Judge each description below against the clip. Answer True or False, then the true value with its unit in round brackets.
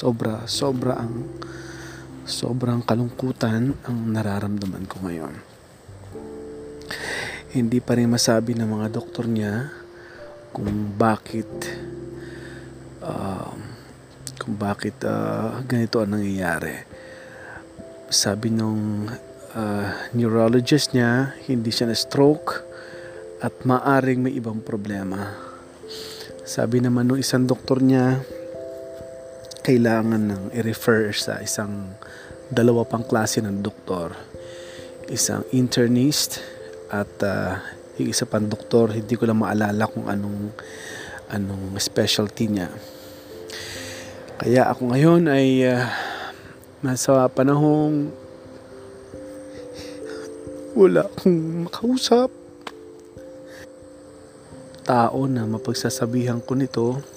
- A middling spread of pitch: True (4.4 semitones)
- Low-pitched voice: True (115 Hz)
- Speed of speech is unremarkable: False (90 wpm)